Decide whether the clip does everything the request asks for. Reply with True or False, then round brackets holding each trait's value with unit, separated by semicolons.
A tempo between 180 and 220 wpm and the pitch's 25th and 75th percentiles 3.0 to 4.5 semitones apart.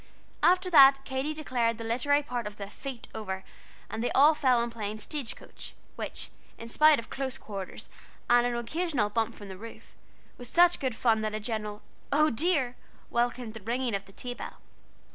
True (185 wpm; 3.9 semitones)